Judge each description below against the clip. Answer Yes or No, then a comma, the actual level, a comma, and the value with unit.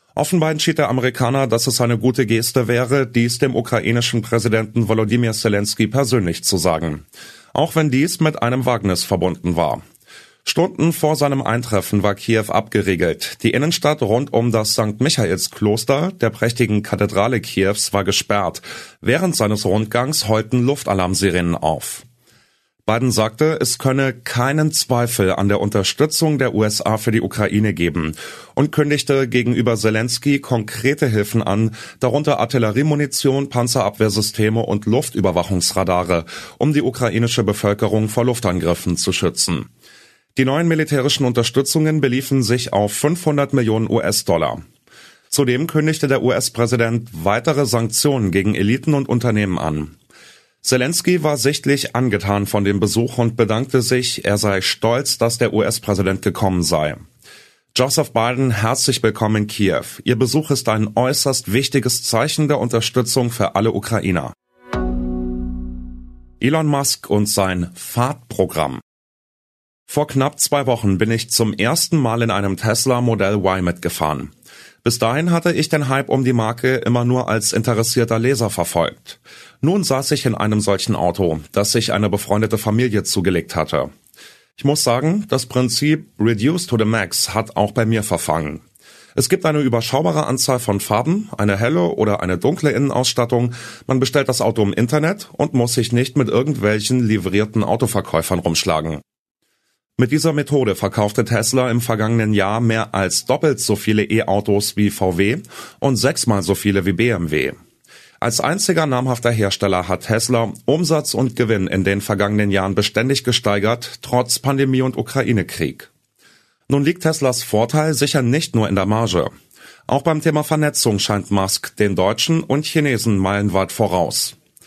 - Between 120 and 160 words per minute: Yes, average, 145 wpm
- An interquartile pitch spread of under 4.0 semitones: No, average, 4.7 semitones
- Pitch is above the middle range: No, low, 115 Hz